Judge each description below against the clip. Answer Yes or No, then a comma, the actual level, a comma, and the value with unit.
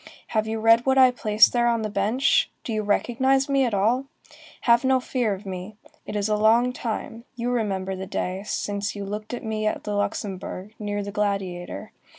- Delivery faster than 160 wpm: Yes, average, 200 wpm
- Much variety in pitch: No, average, 2.9 semitones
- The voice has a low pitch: No, high, 215 Hz